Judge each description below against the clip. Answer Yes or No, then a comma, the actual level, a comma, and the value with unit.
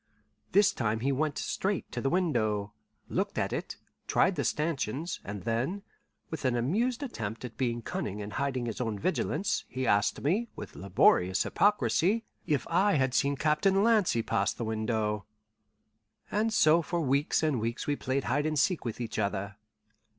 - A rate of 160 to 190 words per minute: Yes, average, 170 wpm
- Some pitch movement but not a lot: No, wide, 7.4 semitones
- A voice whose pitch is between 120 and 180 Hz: Yes, low, 135 Hz